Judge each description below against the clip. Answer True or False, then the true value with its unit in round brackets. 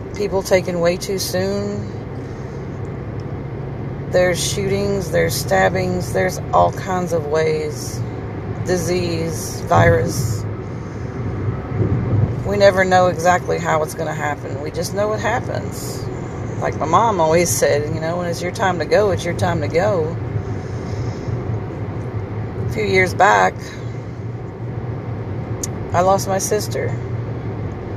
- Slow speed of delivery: True (120 wpm)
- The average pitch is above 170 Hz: False (125 Hz)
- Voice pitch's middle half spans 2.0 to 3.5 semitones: False (5.4 semitones)